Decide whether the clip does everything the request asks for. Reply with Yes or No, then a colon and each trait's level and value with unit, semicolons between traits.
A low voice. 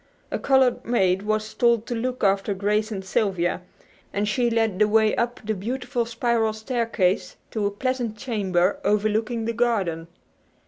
No: high, 220 Hz